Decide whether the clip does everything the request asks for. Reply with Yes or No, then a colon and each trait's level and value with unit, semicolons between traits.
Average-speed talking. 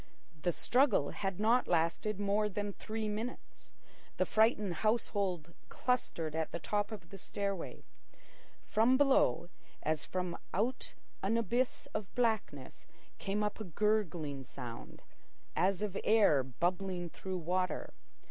No: slow, 130 wpm